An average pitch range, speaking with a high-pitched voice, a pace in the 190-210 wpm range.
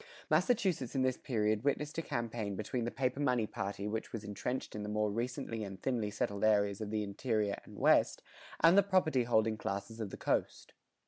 No: average, 3.8 semitones; low, 115 Hz; average, 195 wpm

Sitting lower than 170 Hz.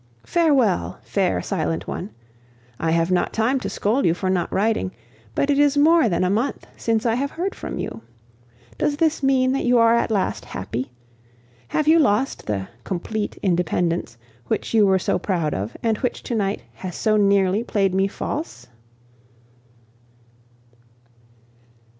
No: high, 210 Hz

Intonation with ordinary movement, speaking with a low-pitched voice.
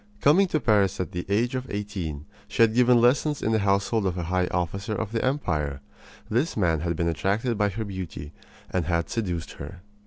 Yes: average, 4.9 semitones; low, 100 Hz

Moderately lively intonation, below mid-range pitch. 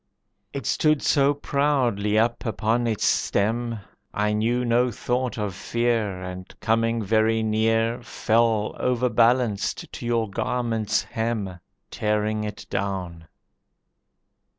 No: narrow, 2.2 semitones; low, 115 Hz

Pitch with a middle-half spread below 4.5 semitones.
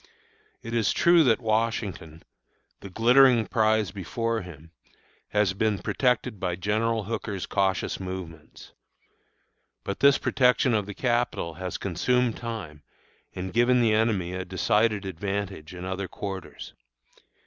Yes: average, 3.7 semitones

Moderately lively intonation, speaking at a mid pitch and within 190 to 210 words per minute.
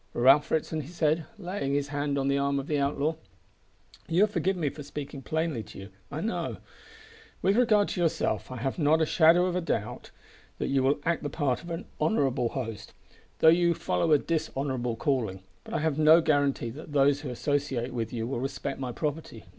Yes: average, 3.4 semitones; medium, 145 Hz; average, 195 wpm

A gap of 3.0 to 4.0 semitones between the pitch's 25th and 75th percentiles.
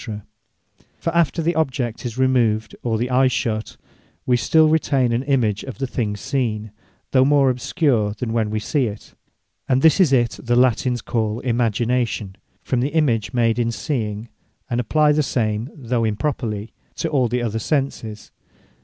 Yes: average, 3.4 semitones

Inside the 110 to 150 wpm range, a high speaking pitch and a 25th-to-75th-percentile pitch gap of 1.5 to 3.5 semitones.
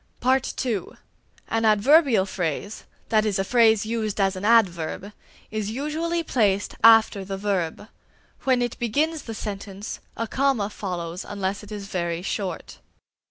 Yes: average, 145 wpm; high, 210 Hz; average, 3.2 semitones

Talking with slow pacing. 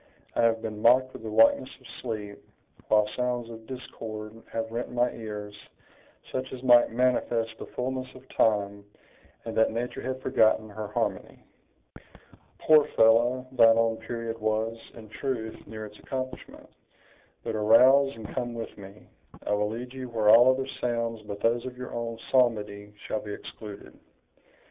No: average, 160 wpm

